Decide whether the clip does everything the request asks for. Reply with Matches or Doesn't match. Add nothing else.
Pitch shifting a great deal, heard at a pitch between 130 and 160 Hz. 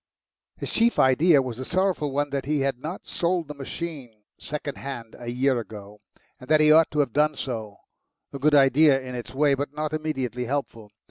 Doesn't match